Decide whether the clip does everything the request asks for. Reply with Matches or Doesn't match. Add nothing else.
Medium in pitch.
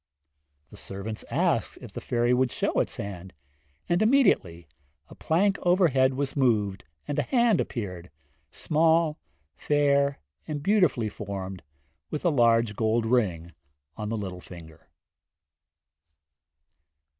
Doesn't match